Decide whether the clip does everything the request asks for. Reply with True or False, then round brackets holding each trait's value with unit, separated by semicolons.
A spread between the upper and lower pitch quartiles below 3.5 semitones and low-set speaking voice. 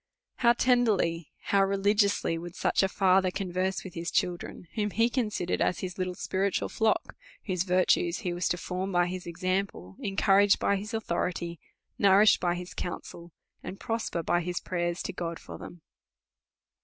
False (2.4 semitones; 185 Hz)